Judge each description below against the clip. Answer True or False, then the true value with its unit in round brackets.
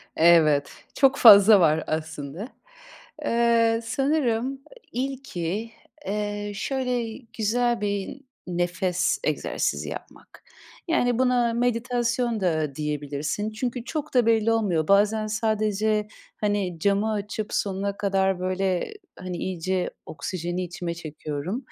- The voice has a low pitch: False (205 Hz)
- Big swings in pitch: False (4.7 semitones)